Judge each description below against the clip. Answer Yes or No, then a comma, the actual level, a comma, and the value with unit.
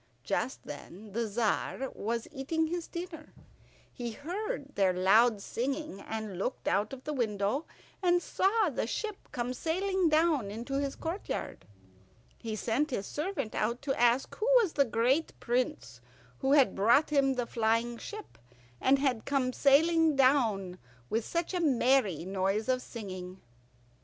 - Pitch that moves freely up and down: Yes, wide, 6.0 semitones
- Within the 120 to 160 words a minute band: Yes, average, 150 wpm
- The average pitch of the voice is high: Yes, very high, 255 Hz